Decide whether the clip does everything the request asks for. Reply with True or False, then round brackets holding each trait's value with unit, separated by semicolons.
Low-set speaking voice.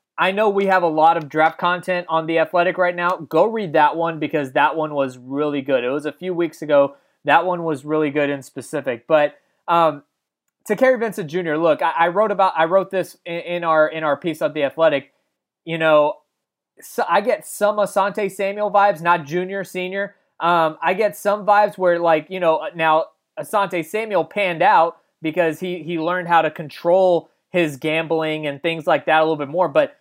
False (170 Hz)